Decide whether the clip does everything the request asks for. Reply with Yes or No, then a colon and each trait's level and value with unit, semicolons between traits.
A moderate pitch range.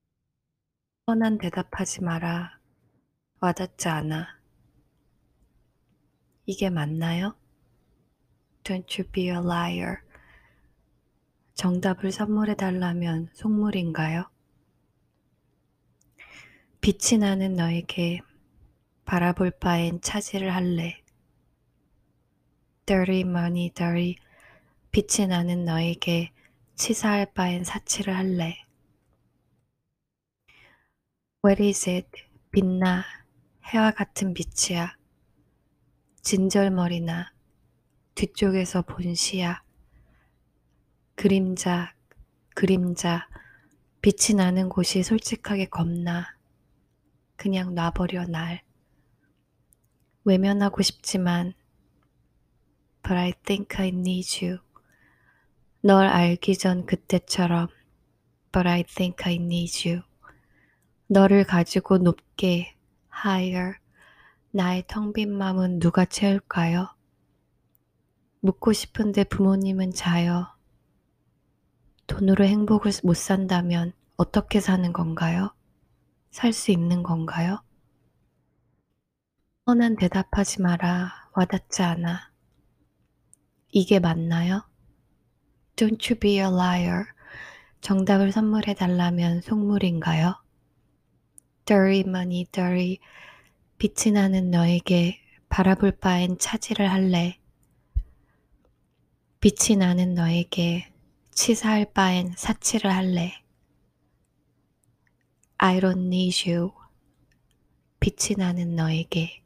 No: narrow, 2.3 semitones